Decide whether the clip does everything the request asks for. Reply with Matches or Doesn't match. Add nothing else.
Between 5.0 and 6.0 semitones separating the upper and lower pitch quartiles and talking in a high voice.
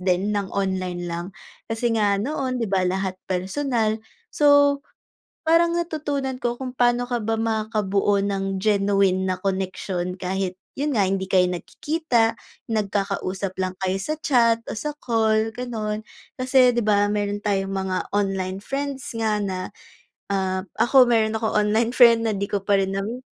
Doesn't match